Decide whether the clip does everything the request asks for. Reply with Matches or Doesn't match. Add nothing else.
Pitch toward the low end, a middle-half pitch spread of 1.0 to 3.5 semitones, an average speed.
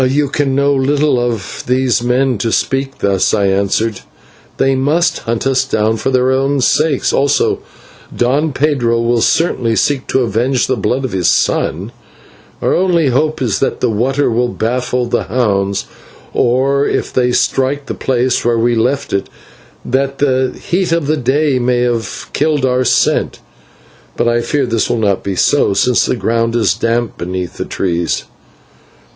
Matches